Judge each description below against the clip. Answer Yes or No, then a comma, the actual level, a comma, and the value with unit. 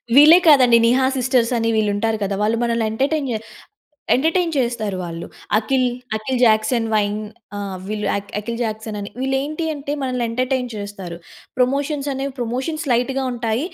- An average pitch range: Yes, average, 3.7 semitones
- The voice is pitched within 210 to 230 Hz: No, high, 240 Hz